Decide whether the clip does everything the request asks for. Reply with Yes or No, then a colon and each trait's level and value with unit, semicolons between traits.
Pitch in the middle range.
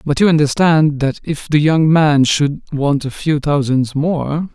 Yes: medium, 150 Hz